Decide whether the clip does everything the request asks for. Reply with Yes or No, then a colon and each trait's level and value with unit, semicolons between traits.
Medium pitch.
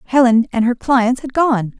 No: high, 245 Hz